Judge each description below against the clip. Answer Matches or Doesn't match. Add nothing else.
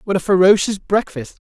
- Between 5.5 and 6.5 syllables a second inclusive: Matches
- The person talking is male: Matches